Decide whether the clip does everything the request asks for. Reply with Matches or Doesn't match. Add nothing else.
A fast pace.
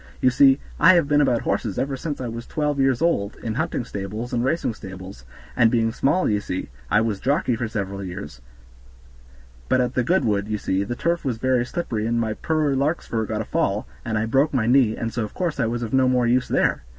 Matches